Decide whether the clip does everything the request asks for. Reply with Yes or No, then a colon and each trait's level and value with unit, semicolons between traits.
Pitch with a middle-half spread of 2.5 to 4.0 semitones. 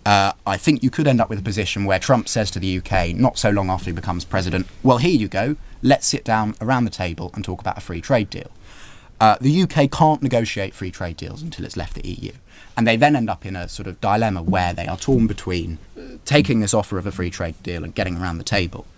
No: average, 4.5 semitones